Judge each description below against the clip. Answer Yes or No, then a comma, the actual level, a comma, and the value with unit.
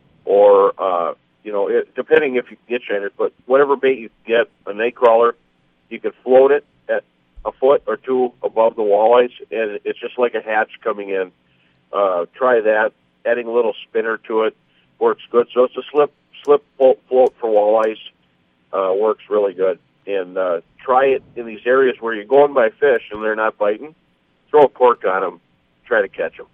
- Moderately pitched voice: No, low, 125 Hz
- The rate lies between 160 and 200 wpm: Yes, average, 195 wpm